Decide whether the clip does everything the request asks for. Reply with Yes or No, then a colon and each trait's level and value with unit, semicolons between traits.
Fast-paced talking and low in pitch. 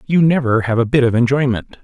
Yes: fast, 230 wpm; low, 130 Hz